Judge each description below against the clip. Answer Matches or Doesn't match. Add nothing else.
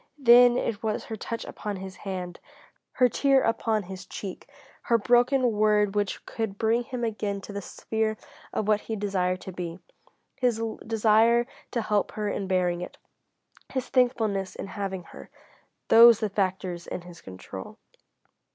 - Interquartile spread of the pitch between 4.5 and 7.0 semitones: Doesn't match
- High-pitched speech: Matches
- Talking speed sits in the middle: Matches